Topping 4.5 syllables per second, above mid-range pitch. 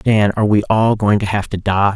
No: 5.4 syllables/s; low, 105 Hz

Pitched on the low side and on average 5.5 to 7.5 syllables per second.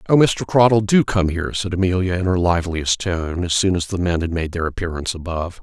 Yes: very low, 90 Hz; 5.9 syllables/s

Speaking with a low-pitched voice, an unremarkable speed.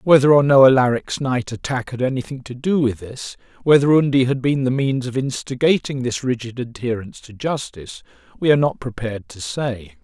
Yes: low, 125 Hz; average, 185 wpm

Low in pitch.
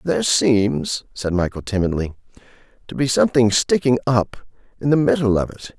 Yes: low, 115 Hz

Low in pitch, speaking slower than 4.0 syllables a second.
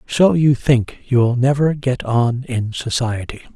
Yes: low, 130 Hz; 3.8 syllables/s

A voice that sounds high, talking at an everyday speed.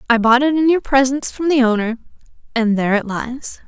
Yes: very high, 250 Hz; average, 195 wpm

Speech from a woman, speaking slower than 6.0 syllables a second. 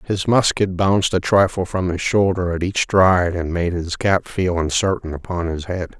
No: male; 4.8 syllables/s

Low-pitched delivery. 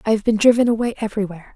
No: high, 215 Hz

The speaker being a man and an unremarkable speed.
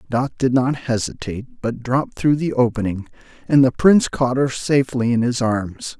Yes: male; average, 180 wpm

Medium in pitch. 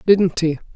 Yes: medium, 175 Hz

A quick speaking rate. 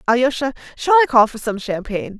No: average, 190 wpm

